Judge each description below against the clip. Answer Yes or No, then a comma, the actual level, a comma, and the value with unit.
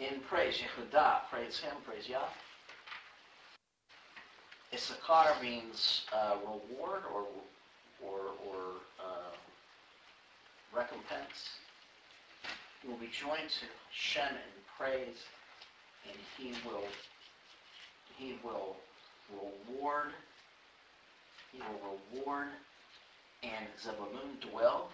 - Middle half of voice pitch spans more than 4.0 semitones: Yes, average, 5.1 semitones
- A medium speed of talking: No, slow, 85 wpm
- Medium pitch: No, low, 120 Hz